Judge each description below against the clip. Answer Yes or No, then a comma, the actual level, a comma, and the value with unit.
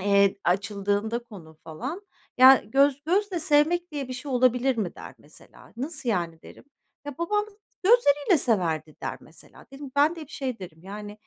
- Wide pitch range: Yes, wide, 6.7 semitones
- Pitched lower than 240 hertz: No, very high, 255 Hz